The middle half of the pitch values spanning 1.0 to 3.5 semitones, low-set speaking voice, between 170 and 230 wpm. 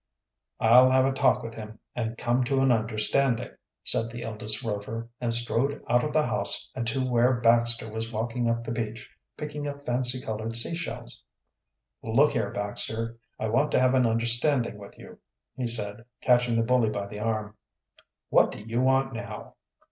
Yes: narrow, 2.4 semitones; low, 115 Hz; average, 180 wpm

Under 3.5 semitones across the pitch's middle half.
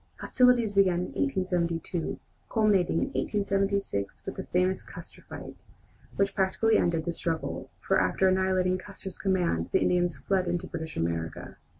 Yes: narrow, 2.6 semitones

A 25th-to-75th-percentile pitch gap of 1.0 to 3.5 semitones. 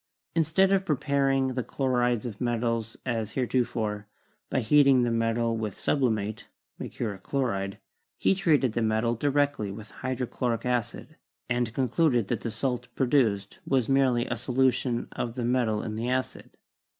Yes: average, 2.9 semitones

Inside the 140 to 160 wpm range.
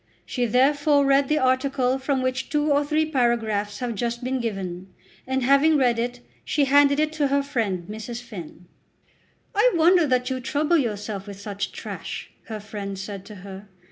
No: average, 175 wpm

